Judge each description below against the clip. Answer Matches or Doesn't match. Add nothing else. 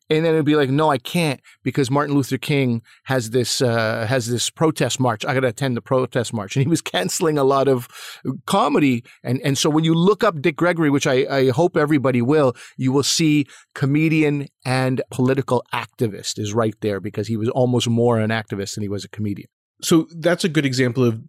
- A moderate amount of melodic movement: Matches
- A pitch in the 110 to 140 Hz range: Matches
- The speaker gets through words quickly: Matches